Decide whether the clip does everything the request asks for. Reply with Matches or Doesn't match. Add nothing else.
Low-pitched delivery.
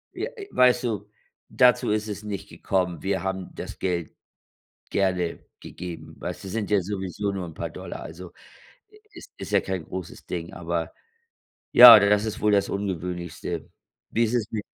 Matches